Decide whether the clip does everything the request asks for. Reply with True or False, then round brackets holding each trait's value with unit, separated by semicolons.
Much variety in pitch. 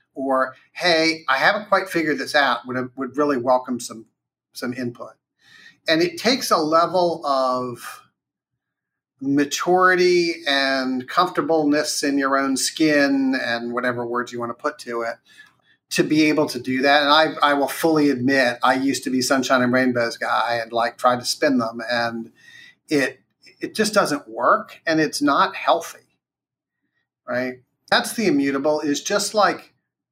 False (4.4 semitones)